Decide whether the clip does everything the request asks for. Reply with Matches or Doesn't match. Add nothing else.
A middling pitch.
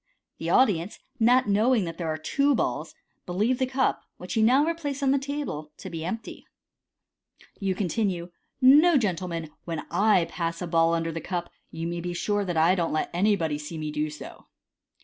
Matches